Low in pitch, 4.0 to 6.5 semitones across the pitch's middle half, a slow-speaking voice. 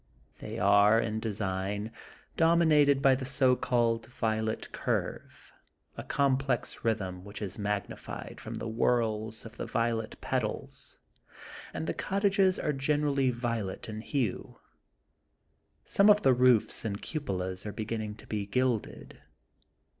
Yes: low, 115 Hz; average, 4.3 semitones; slow, 130 wpm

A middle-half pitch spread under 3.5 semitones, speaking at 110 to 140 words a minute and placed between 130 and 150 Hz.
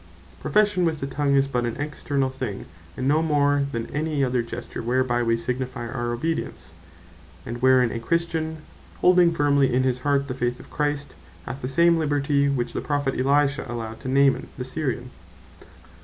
No: average, 2.9 semitones; average, 175 wpm; low, 135 Hz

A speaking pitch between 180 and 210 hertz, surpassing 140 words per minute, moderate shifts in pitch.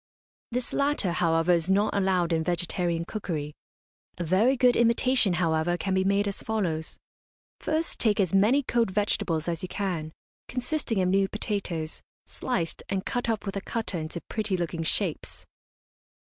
Yes: high, 190 Hz; average, 160 wpm; average, 4.4 semitones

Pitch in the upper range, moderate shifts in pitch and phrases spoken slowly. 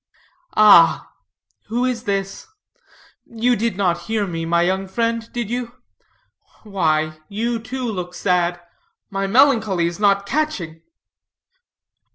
Yes: high, 200 Hz; average, 4.7 semitones; slow, 120 wpm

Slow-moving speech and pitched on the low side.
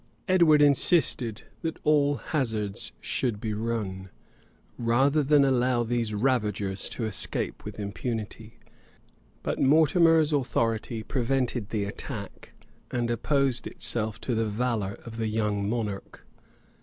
Yes: slow, 120 wpm; low, 115 Hz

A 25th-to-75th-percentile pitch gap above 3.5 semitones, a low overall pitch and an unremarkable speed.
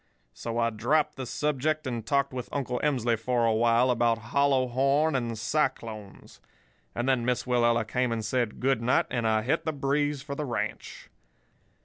No: average, 3.0 semitones; low, 125 Hz; average, 175 wpm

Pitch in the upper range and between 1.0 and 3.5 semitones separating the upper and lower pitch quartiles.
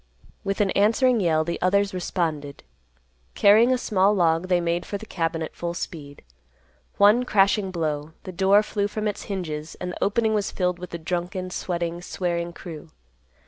No: medium, 180 Hz; average, 3.1 semitones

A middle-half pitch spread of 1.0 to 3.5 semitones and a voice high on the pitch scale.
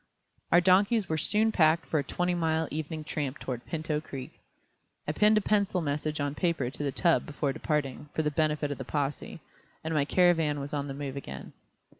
No: average, 3.0 semitones; medium, 155 Hz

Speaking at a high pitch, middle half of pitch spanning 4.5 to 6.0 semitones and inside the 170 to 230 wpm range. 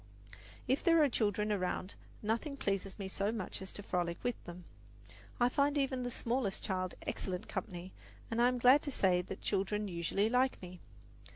Yes: high, 210 Hz; average, 5.0 semitones; average, 180 wpm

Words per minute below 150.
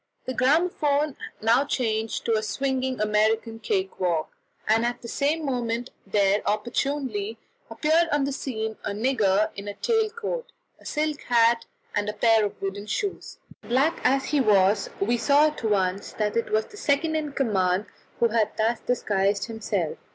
No: average, 165 wpm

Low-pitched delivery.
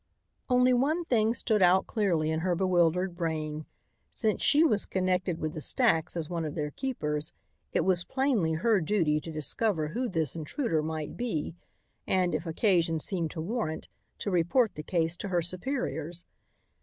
No: medium, 175 Hz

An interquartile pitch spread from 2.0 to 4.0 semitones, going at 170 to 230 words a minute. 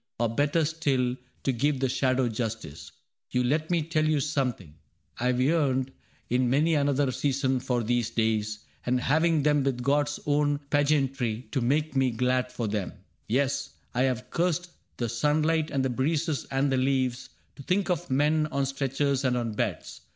Yes: average, 3.0 semitones; average, 175 wpm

